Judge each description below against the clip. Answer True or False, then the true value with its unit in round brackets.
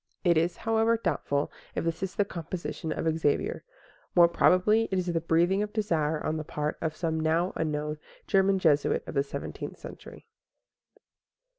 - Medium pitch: True (165 Hz)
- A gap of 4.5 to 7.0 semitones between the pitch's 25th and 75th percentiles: False (3.6 semitones)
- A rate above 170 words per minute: False (165 wpm)